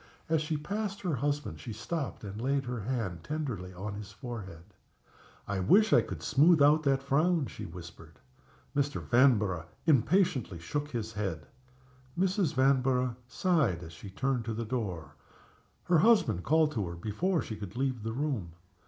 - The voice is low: Yes, low, 125 Hz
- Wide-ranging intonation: Yes, wide, 6.8 semitones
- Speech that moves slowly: No, average, 160 wpm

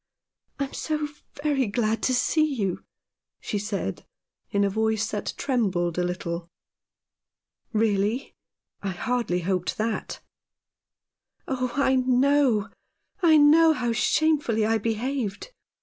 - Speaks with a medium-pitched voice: No, high, 225 Hz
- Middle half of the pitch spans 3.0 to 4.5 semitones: No, average, 5.2 semitones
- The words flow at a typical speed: No, slow, 130 wpm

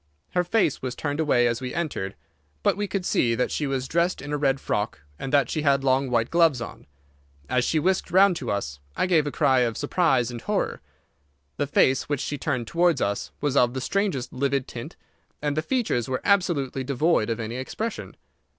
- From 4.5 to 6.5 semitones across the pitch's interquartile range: Yes, average, 5.0 semitones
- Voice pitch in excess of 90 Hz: Yes, medium, 140 Hz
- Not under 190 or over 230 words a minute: Yes, fast, 205 wpm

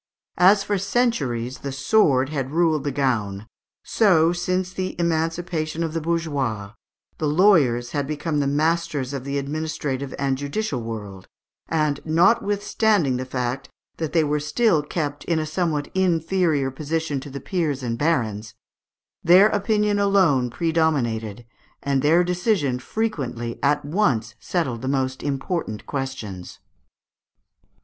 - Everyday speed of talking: No, slow, 130 wpm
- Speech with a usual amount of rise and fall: Yes, average, 4.7 semitones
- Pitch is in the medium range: Yes, medium, 150 Hz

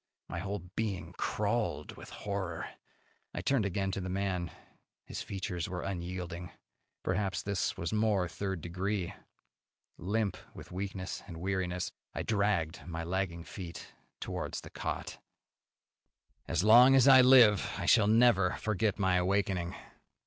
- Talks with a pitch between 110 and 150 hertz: No, very low, 95 Hz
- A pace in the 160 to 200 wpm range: No, slow, 135 wpm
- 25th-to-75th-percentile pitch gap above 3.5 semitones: No, average, 2.7 semitones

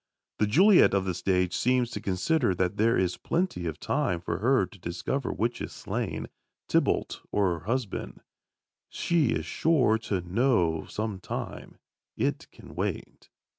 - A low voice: Yes, low, 105 Hz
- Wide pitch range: Yes, wide, 5.8 semitones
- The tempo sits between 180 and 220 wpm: No, average, 155 wpm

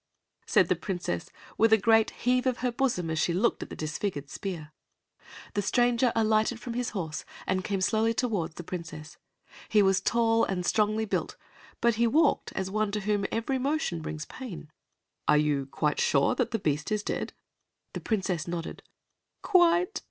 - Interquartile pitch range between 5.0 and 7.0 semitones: Yes, wide, 5.6 semitones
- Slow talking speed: No, average, 175 wpm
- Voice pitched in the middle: No, high, 210 Hz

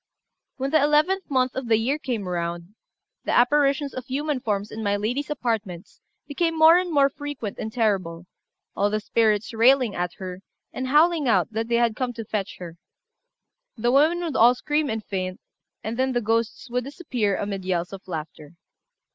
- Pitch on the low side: No, high, 235 Hz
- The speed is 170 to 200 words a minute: Yes, average, 180 wpm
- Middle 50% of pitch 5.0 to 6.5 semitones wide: Yes, wide, 5.6 semitones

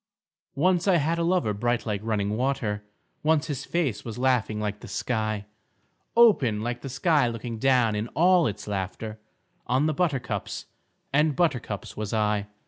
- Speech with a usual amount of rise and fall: No, wide, 6.0 semitones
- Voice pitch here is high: No, low, 120 Hz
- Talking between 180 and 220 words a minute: No, average, 160 wpm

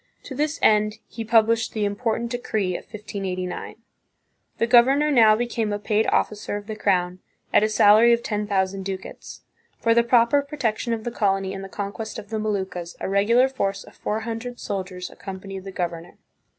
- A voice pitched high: Yes, high, 215 Hz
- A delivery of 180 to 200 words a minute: Yes, average, 190 wpm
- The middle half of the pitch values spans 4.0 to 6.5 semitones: No, average, 3.1 semitones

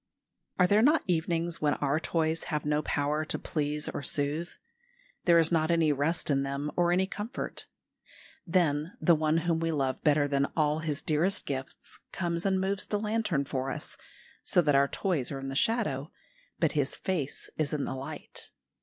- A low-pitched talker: No, medium, 155 Hz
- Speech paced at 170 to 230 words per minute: Yes, average, 185 wpm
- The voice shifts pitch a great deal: No, average, 3.3 semitones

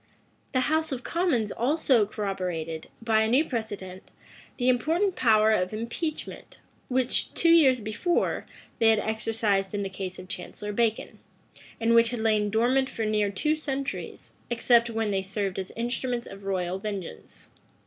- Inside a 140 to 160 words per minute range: Yes, average, 155 wpm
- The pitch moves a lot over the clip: No, average, 4.1 semitones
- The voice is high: Yes, high, 220 Hz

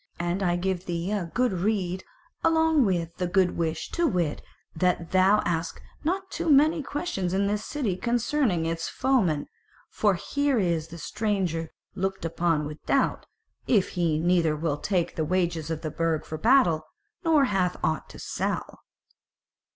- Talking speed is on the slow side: No, average, 160 wpm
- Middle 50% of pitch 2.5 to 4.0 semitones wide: No, average, 5.0 semitones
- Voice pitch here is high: No, medium, 180 Hz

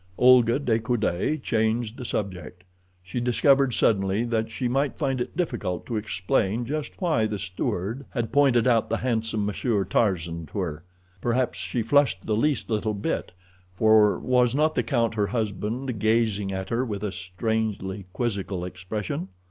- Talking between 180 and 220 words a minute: No, average, 160 wpm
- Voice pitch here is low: Yes, low, 110 Hz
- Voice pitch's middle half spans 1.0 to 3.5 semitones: No, average, 3.9 semitones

